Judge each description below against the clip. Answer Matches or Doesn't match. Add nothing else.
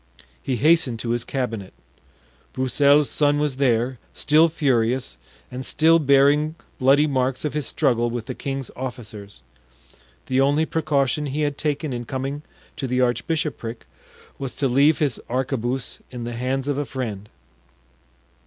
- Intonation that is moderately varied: Matches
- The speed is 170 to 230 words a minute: Doesn't match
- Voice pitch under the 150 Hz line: Matches